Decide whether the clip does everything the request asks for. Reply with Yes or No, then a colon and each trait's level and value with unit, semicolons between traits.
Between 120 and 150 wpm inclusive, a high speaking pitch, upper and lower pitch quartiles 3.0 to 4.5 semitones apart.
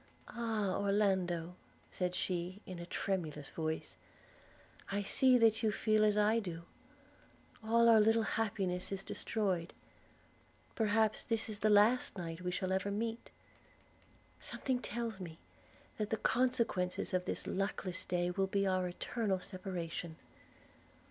Yes: slow, 135 wpm; high, 195 Hz; average, 3.5 semitones